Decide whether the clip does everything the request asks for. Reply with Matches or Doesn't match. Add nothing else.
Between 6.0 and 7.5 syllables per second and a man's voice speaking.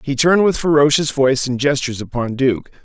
Matches